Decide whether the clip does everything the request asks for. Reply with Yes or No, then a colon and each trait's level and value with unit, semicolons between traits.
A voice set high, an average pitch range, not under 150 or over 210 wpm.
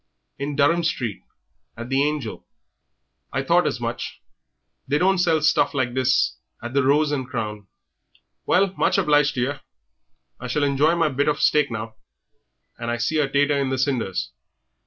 No: medium, 140 Hz; average, 3.1 semitones; average, 170 wpm